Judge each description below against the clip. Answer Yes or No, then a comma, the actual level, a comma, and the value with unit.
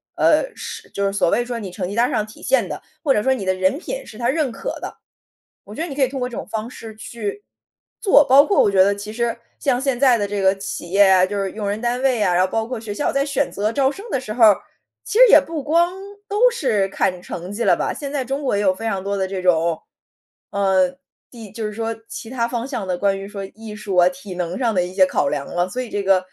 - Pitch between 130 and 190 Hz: No, high, 215 Hz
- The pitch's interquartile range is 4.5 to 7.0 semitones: Yes, average, 4.9 semitones